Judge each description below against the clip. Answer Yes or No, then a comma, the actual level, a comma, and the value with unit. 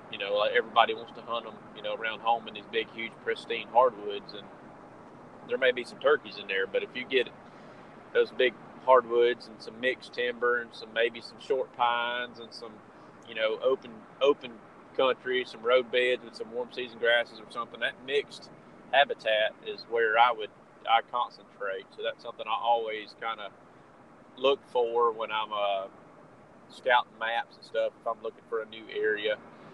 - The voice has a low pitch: Yes, low, 130 Hz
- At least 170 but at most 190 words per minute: Yes, average, 185 wpm